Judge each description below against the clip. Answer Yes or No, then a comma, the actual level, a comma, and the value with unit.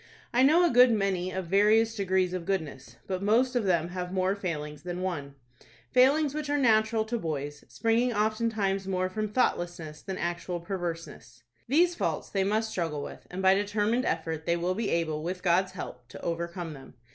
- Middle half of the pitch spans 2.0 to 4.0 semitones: No, average, 4.6 semitones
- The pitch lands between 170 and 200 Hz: Yes, medium, 185 Hz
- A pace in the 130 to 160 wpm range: No, average, 180 wpm